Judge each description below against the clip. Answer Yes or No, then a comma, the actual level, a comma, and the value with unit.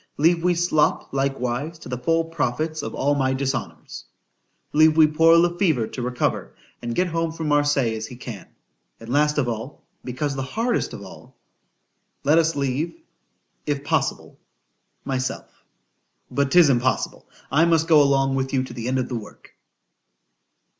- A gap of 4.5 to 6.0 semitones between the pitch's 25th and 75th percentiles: No, average, 4.0 semitones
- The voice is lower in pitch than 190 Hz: Yes, medium, 140 Hz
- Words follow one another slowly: No, average, 155 wpm